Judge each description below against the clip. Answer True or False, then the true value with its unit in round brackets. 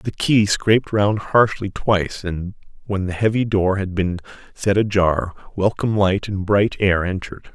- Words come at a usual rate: True (165 wpm)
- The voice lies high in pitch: False (100 Hz)